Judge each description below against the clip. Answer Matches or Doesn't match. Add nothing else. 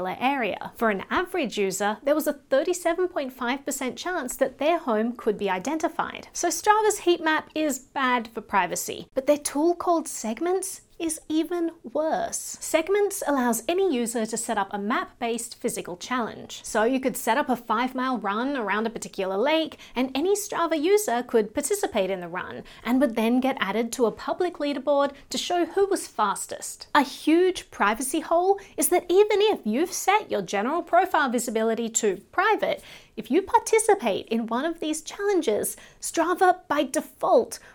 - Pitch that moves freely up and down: Matches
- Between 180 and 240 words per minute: Doesn't match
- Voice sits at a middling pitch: Doesn't match